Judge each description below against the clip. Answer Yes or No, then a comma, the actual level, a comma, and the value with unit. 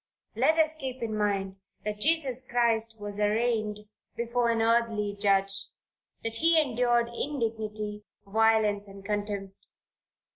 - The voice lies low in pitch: No, high, 225 Hz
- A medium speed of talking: No, slow, 120 wpm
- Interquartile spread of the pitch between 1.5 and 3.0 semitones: Yes, narrow, 2.5 semitones